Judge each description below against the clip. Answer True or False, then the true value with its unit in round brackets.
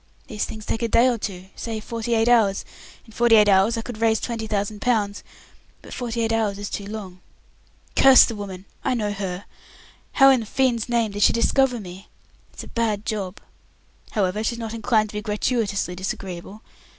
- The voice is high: True (215 Hz)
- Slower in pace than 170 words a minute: False (195 wpm)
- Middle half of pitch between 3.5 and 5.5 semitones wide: False (2.4 semitones)